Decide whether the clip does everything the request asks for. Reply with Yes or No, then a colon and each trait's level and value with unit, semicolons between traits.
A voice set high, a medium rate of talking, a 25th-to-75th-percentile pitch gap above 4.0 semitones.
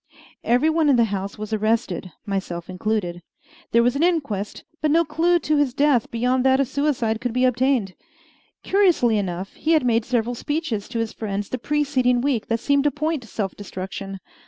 Yes: high, 245 Hz; average, 190 wpm; wide, 5.4 semitones